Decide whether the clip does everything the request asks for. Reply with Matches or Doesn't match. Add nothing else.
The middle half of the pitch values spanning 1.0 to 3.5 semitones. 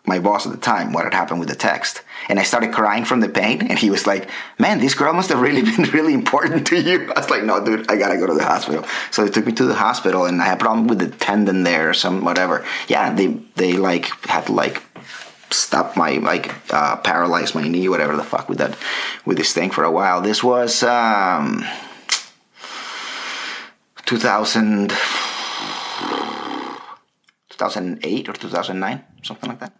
Doesn't match